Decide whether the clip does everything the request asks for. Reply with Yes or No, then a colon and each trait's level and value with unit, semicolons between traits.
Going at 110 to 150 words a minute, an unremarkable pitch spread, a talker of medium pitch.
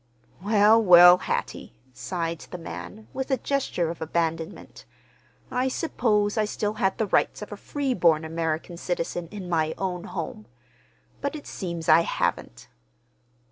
Yes: average, 140 wpm; average, 4.4 semitones; medium, 180 Hz